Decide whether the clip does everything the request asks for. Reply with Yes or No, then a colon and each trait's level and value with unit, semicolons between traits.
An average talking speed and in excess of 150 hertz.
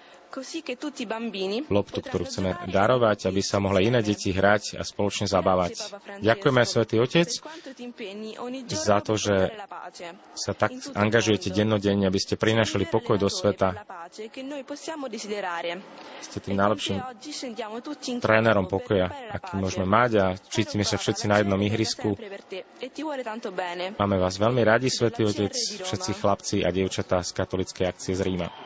No: average, 125 wpm; low, 110 Hz